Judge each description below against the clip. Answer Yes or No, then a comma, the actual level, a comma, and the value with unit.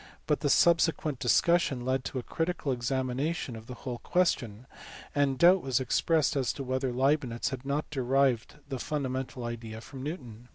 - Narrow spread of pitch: No, average, 3.1 semitones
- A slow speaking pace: No, average, 165 wpm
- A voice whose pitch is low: Yes, low, 130 Hz